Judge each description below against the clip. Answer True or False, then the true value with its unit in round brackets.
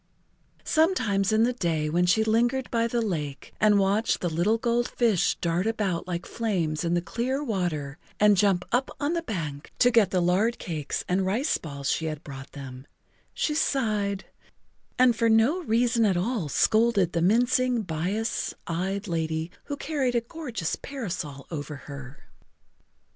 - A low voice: False (200 Hz)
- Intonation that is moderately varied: False (5.9 semitones)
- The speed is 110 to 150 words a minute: False (165 wpm)